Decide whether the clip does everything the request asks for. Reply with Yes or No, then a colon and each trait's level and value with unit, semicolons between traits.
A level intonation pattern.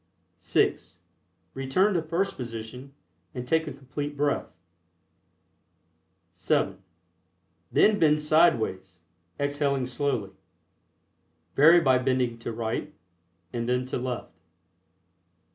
No: average, 3.6 semitones